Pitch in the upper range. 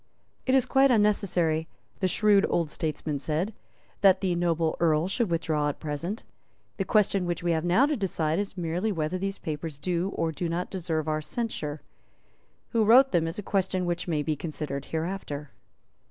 No: medium, 175 Hz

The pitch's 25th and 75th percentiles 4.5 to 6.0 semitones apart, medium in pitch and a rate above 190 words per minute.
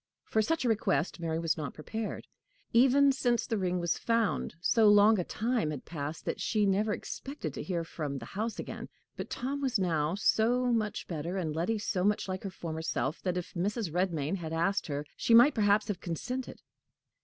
No: wide, 5.4 semitones; high, 195 Hz; average, 200 wpm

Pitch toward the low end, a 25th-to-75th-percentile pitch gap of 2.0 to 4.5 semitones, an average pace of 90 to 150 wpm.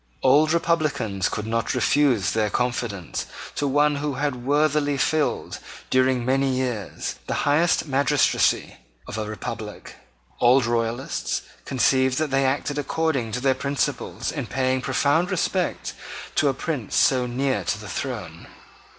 Yes: low, 130 Hz; average, 3.3 semitones; average, 140 wpm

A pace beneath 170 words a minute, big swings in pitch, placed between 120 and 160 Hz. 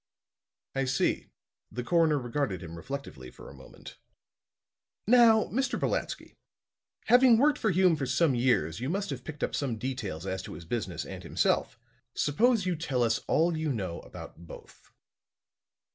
Yes: average, 160 wpm; wide, 8.2 semitones; low, 135 Hz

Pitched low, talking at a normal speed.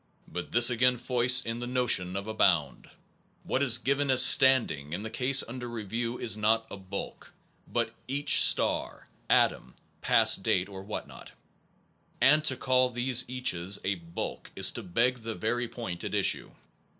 Yes: low, 120 Hz; average, 170 wpm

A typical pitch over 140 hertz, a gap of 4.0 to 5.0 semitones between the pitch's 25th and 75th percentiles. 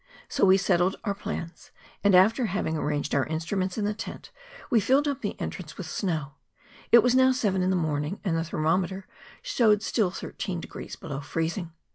Yes: medium, 185 Hz; average, 4.4 semitones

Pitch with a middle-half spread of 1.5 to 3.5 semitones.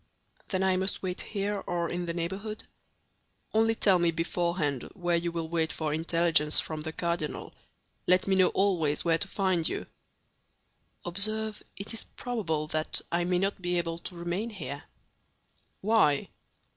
Yes: average, 2.8 semitones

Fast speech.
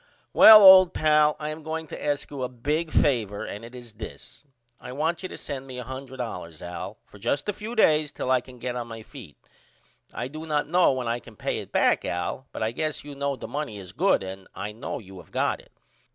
Yes: fast, 235 wpm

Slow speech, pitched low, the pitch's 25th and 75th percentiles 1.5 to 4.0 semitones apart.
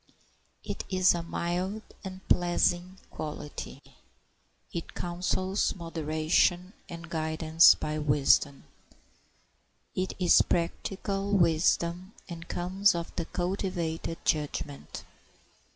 No: slow, 90 wpm; medium, 175 Hz; narrow, 2.5 semitones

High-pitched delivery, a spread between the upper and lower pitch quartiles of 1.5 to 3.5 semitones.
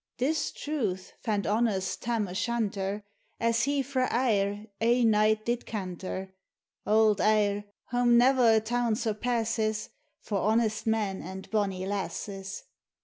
Yes: high, 215 Hz; average, 2.9 semitones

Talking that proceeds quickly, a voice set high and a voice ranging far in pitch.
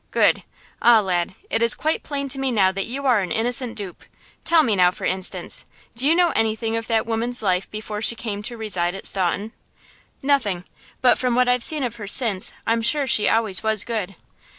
No: fast, 210 wpm; high, 225 Hz; average, 3.8 semitones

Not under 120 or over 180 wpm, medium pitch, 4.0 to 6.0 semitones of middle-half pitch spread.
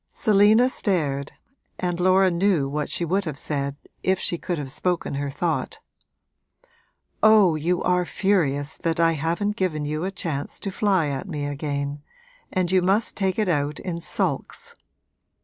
Yes: average, 160 wpm; medium, 170 Hz; average, 4.5 semitones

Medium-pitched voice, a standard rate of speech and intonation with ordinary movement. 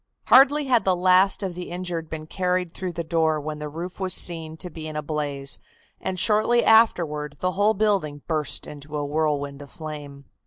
Yes: medium, 165 Hz; average, 195 wpm; average, 3.6 semitones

